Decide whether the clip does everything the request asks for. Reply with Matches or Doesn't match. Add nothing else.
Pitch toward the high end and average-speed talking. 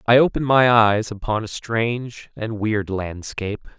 Doesn't match